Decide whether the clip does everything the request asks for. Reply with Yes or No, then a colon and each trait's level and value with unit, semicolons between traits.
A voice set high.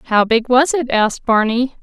Yes: high, 240 Hz